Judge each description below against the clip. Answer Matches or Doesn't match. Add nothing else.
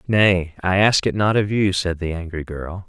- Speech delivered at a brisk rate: Matches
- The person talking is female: Doesn't match